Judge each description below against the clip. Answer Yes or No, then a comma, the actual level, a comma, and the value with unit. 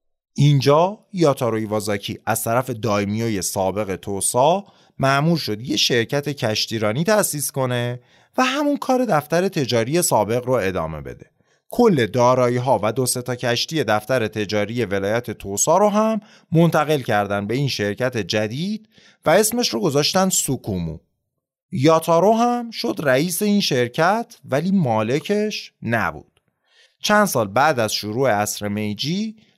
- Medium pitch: No, low, 130 Hz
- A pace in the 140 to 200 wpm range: No, average, 130 wpm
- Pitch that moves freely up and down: Yes, wide, 8.7 semitones